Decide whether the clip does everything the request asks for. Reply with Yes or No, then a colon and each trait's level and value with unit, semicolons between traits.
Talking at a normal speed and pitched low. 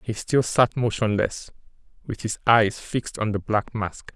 Yes: average, 175 wpm; low, 110 Hz